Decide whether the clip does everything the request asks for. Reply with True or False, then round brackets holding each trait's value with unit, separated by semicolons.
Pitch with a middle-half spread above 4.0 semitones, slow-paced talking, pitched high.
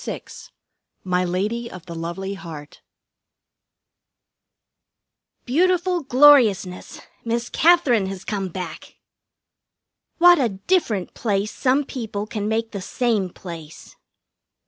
True (5.5 semitones; 100 wpm; 210 Hz)